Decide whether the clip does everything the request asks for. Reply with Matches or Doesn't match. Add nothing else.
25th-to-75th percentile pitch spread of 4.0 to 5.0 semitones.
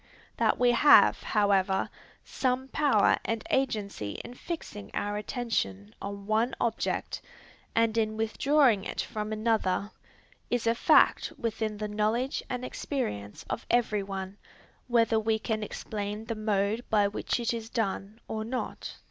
Doesn't match